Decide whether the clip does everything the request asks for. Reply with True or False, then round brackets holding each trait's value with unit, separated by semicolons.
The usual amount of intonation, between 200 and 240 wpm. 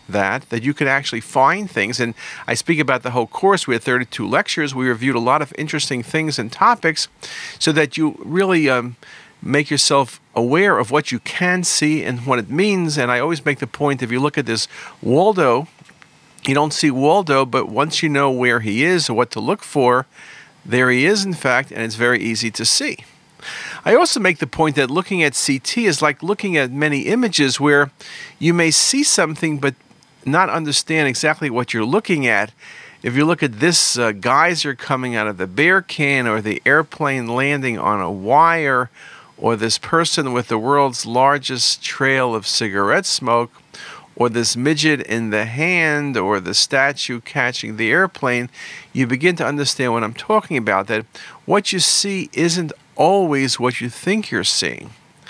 False (4.5 semitones; 190 wpm)